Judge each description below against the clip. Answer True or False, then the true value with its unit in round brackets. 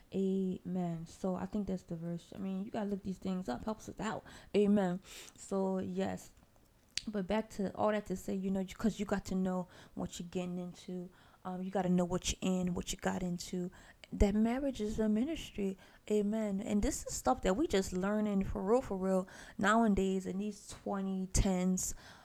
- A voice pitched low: False (195 Hz)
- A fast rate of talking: False (195 wpm)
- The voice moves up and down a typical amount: False (2.1 semitones)